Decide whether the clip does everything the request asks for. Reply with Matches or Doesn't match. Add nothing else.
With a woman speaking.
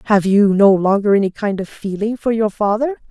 Matches